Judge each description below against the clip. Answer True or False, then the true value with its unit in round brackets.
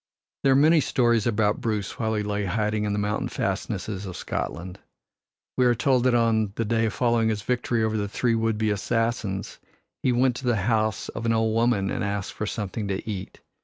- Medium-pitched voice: False (110 Hz)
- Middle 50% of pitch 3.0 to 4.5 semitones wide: False (2.4 semitones)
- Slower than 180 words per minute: False (205 wpm)